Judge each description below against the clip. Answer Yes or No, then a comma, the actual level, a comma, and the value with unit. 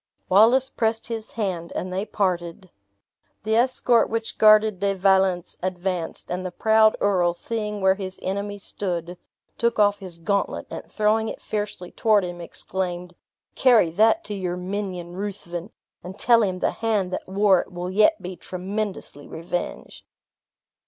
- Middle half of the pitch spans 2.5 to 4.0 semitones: Yes, average, 3.1 semitones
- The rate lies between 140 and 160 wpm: Yes, average, 150 wpm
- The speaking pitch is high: Yes, high, 195 Hz